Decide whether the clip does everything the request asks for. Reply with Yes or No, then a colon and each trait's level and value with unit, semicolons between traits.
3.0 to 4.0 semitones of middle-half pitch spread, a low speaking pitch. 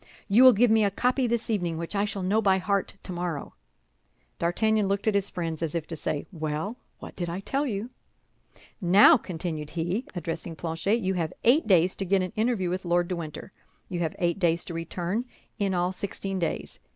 No: average, 3.4 semitones; medium, 185 Hz